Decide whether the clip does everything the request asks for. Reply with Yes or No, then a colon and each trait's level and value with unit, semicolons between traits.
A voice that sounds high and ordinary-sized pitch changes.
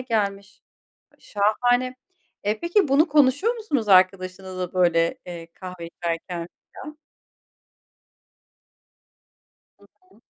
No: high, 200 Hz; wide, 6.2 semitones